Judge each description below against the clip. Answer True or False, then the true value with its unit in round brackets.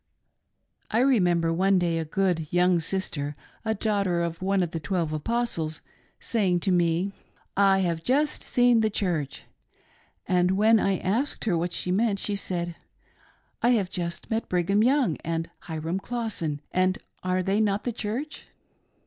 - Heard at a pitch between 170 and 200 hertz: True (185 Hz)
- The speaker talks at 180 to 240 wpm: False (170 wpm)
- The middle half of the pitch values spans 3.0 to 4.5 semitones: True (4.1 semitones)